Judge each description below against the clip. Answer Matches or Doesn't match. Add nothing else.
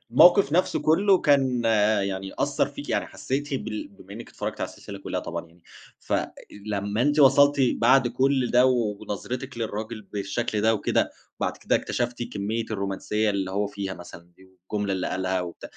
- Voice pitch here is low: Matches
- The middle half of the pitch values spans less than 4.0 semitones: Doesn't match